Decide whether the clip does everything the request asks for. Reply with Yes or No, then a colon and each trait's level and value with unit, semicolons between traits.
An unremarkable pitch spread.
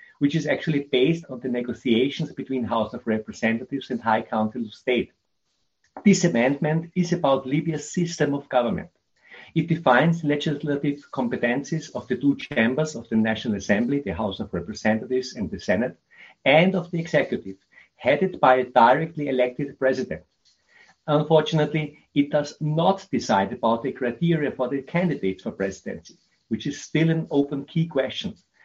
Yes: average, 4.4 semitones